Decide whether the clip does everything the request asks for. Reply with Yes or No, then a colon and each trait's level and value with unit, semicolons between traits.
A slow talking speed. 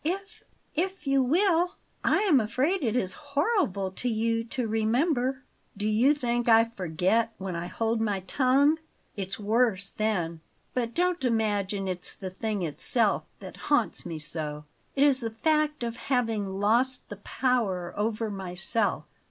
No: average, 150 wpm